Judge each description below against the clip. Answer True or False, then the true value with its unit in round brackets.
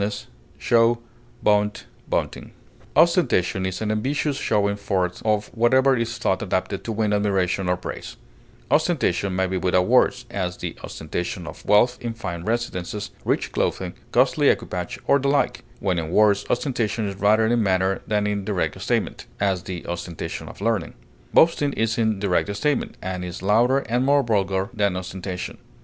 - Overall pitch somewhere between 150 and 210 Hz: False (105 Hz)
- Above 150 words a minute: True (160 wpm)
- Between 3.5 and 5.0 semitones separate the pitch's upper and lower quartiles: True (4.0 semitones)